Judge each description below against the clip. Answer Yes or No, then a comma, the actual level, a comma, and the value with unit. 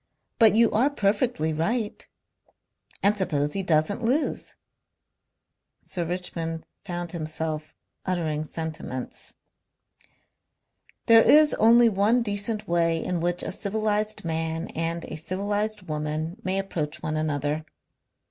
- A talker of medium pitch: Yes, medium, 175 Hz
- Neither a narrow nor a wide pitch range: Yes, average, 4.9 semitones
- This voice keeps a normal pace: No, slow, 115 wpm